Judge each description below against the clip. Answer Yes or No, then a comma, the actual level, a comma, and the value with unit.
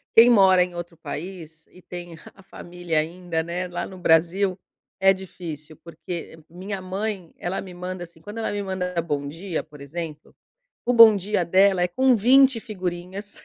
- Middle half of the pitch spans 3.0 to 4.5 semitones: No, narrow, 2.5 semitones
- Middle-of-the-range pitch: Yes, medium, 180 Hz